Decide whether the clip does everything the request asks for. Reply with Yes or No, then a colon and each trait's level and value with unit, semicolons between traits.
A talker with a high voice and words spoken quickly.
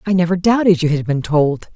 No: medium, 170 Hz; fast, 240 wpm